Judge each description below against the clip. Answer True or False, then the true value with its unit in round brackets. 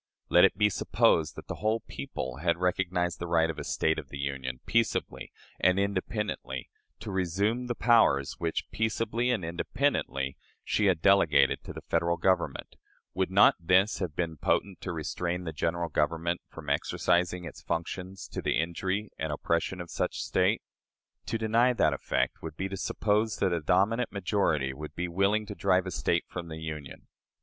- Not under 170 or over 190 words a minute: True (175 wpm)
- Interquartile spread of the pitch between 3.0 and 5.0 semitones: True (3.8 semitones)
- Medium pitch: False (90 Hz)